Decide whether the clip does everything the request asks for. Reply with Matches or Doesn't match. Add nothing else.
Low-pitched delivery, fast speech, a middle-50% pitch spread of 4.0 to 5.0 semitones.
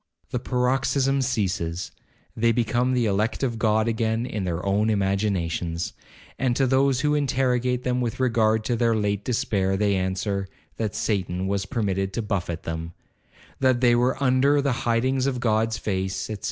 Doesn't match